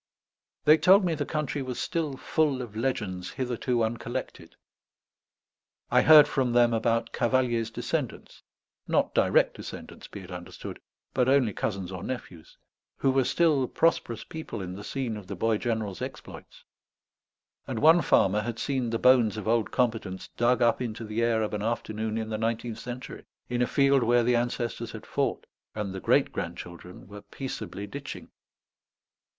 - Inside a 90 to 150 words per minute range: No, average, 165 wpm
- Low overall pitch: Yes, low, 120 Hz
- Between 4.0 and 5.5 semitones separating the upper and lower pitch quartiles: No, average, 3.3 semitones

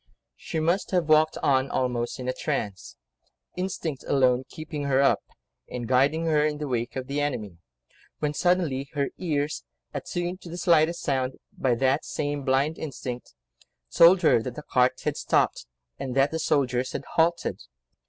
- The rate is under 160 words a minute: No, average, 165 wpm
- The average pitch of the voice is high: No, medium, 140 Hz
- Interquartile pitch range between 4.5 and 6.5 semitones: No, average, 3.7 semitones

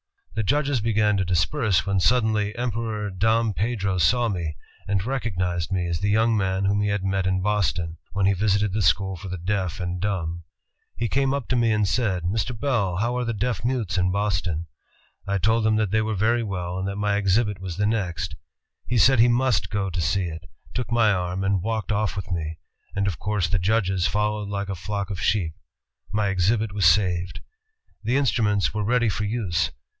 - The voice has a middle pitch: No, low, 100 Hz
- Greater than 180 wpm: Yes, fast, 205 wpm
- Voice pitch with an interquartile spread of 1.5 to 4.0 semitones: Yes, average, 3.1 semitones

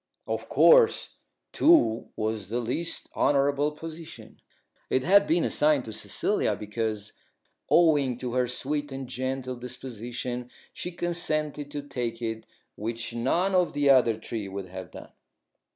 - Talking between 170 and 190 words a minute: No, slow, 135 wpm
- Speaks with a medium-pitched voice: No, low, 130 Hz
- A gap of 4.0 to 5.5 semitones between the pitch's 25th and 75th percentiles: Yes, average, 4.6 semitones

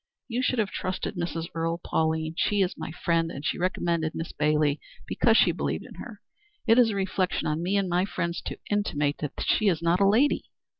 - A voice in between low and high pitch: Yes, medium, 175 Hz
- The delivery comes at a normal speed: No, fast, 210 wpm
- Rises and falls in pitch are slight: No, average, 3.7 semitones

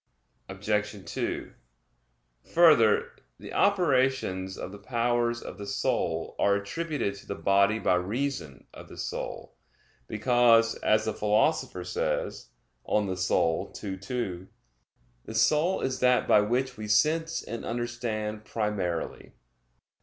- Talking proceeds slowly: Yes, slow, 125 wpm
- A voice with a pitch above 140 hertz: No, low, 110 Hz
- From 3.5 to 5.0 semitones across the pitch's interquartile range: Yes, average, 3.9 semitones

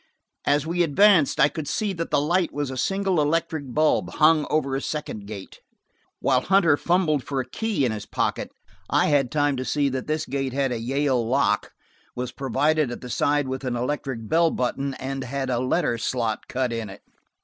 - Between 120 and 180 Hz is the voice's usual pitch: Yes, medium, 140 Hz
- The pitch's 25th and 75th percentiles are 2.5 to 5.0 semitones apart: Yes, average, 3.4 semitones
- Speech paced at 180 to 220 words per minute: Yes, average, 200 wpm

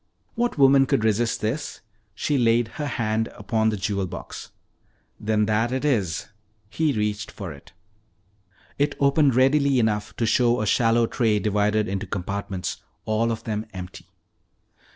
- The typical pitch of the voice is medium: No, low, 110 Hz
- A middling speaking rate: Yes, average, 150 wpm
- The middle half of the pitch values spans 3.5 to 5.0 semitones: Yes, average, 3.8 semitones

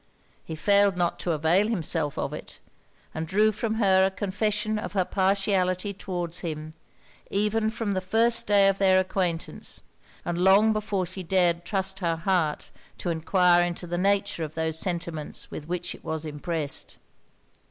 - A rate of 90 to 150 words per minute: No, average, 165 wpm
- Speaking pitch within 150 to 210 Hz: Yes, medium, 185 Hz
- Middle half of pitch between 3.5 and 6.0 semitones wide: No, average, 3.0 semitones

